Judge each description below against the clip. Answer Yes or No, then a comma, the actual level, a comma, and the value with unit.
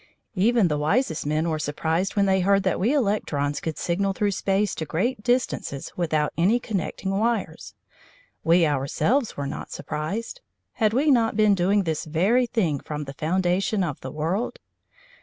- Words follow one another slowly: No, average, 165 wpm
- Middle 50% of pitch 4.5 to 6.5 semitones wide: Yes, wide, 5.4 semitones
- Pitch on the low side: No, high, 190 Hz